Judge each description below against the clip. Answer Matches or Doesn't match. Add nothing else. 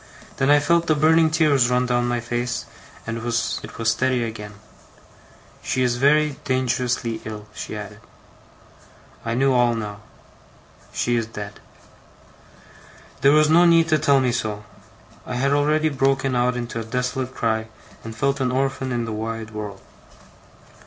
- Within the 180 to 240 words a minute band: Doesn't match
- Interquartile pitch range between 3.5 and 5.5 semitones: Doesn't match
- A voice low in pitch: Matches